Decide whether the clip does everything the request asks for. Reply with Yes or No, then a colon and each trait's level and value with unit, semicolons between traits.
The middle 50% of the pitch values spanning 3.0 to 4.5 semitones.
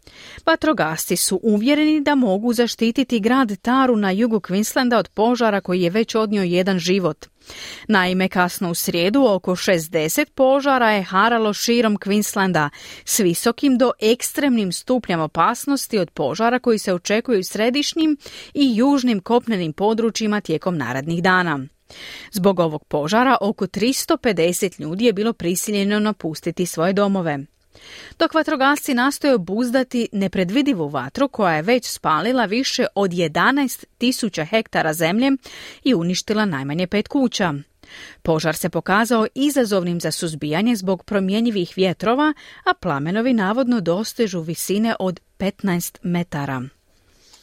No: average, 5.2 semitones